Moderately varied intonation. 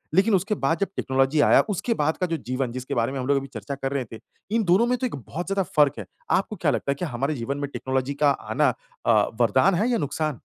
No: wide, 6.3 semitones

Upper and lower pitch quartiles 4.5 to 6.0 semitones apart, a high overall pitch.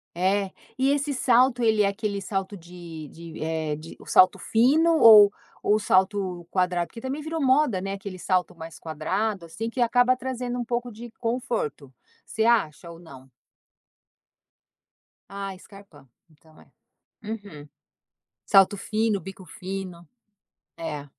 Yes: average, 5.3 semitones; high, 195 Hz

